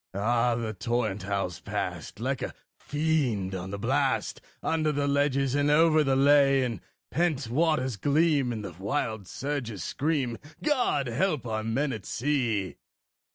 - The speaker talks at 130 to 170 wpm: Yes, average, 155 wpm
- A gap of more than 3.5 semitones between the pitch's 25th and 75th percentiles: Yes, average, 5.1 semitones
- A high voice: No, low, 130 Hz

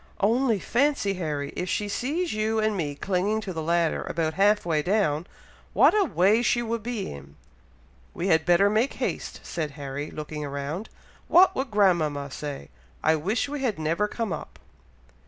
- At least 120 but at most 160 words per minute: No, average, 175 wpm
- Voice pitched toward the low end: No, medium, 185 Hz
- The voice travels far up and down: Yes, wide, 6.0 semitones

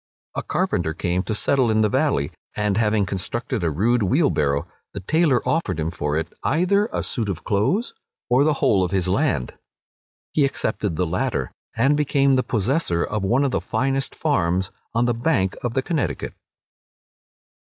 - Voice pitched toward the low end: Yes, low, 110 Hz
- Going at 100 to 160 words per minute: No, average, 175 wpm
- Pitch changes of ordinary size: No, wide, 6.9 semitones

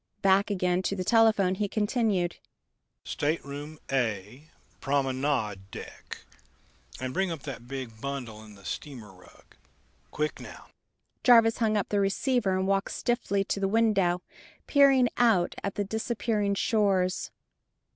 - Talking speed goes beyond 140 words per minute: No, slow, 135 wpm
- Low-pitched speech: No, medium, 185 Hz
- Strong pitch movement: Yes, wide, 7.2 semitones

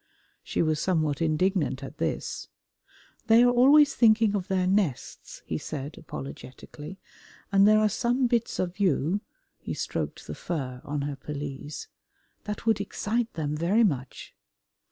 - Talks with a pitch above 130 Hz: Yes, medium, 185 Hz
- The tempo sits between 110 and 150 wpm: Yes, average, 145 wpm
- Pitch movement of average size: No, wide, 6.5 semitones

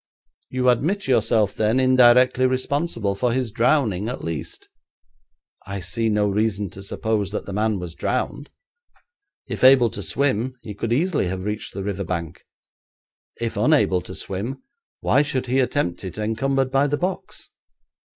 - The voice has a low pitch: Yes, low, 115 Hz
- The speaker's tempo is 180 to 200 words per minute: No, average, 155 wpm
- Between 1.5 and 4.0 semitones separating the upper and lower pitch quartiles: No, average, 4.7 semitones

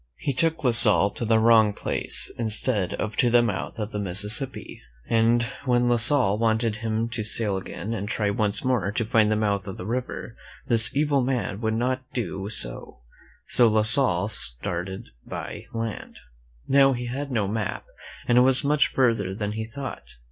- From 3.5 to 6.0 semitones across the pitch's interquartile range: No, average, 2.9 semitones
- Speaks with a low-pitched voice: Yes, low, 115 Hz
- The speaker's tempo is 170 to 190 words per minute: Yes, average, 185 wpm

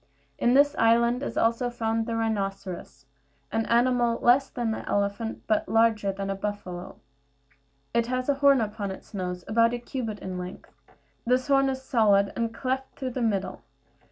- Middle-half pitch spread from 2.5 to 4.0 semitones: Yes, average, 3.6 semitones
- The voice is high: Yes, high, 225 Hz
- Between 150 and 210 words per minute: Yes, average, 170 wpm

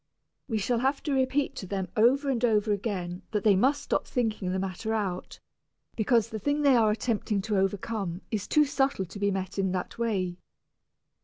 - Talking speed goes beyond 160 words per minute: Yes, average, 190 wpm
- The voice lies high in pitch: Yes, high, 215 Hz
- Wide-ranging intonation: No, average, 4.3 semitones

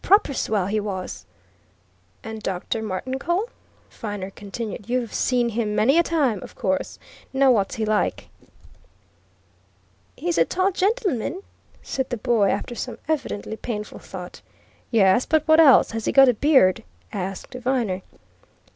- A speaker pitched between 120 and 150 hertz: No, high, 235 Hz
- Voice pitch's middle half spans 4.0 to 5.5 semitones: Yes, average, 5.0 semitones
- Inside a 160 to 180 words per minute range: No, average, 140 wpm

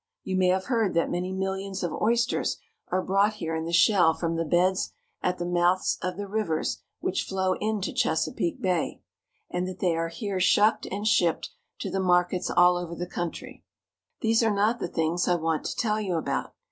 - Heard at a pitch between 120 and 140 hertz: No, medium, 185 Hz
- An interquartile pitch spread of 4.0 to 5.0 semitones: No, average, 2.7 semitones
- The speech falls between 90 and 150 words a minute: No, average, 200 wpm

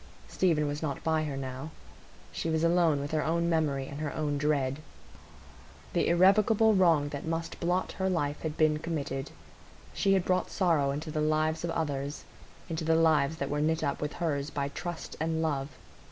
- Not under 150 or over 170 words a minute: No, average, 180 wpm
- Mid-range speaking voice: Yes, medium, 155 Hz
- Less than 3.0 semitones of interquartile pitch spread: Yes, narrow, 2.5 semitones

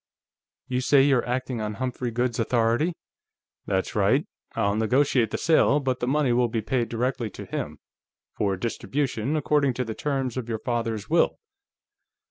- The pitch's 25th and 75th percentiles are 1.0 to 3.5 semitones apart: Yes, average, 2.8 semitones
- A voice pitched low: Yes, low, 125 Hz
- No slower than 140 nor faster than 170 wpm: Yes, average, 160 wpm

